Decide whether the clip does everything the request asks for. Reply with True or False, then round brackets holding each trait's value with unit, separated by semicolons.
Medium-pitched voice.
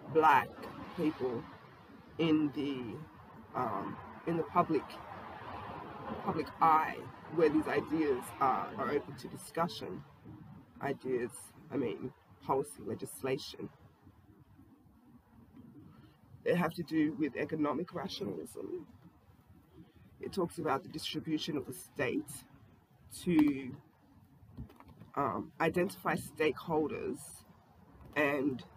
True (155 Hz)